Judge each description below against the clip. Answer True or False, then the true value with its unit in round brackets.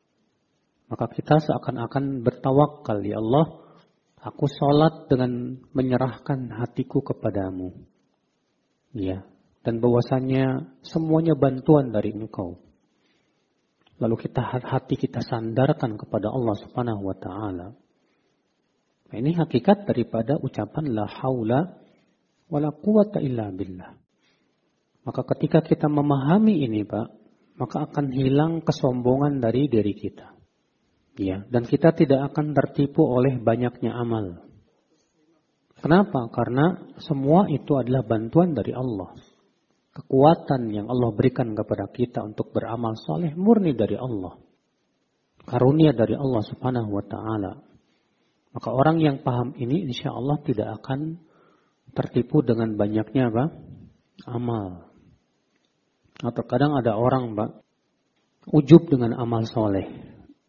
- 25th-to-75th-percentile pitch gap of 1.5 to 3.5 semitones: False (4.6 semitones)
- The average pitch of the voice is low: True (130 Hz)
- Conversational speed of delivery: True (110 wpm)